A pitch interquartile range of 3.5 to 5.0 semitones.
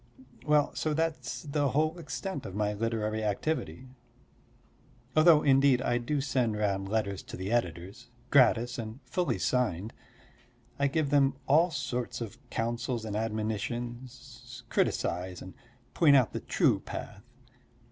Yes: average, 4.5 semitones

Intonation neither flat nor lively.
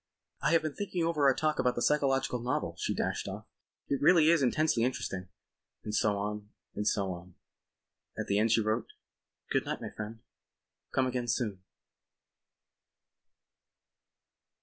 No: wide, 5.7 semitones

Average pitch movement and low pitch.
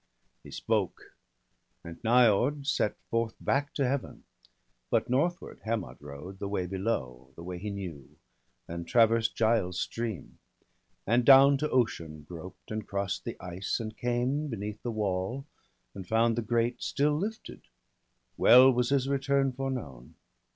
No: wide, 5.7 semitones; low, 115 Hz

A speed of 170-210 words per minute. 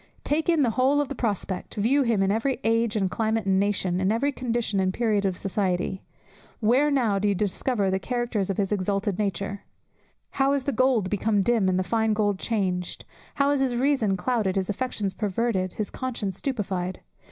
Yes: average, 195 wpm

